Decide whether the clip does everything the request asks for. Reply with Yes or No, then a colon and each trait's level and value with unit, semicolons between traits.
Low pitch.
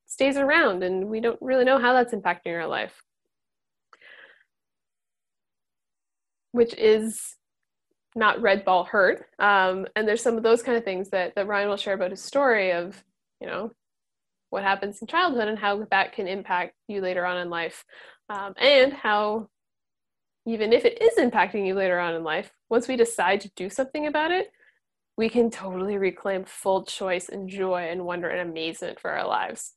No: high, 200 Hz